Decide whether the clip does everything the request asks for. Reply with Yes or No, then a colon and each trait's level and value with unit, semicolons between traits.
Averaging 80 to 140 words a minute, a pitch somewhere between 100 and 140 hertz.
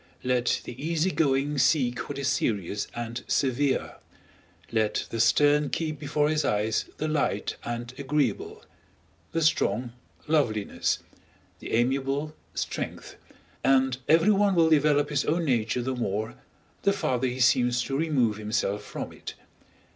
Yes: slow, 135 wpm; low, 135 Hz